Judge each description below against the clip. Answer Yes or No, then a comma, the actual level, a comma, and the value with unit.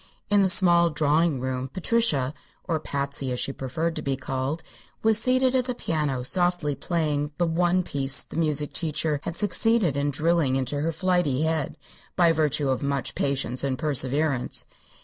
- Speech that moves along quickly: No, average, 170 wpm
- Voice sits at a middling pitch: Yes, medium, 150 Hz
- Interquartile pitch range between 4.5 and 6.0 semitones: No, average, 3.9 semitones